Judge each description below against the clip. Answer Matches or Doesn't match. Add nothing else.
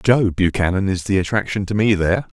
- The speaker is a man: Matches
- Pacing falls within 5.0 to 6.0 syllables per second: Matches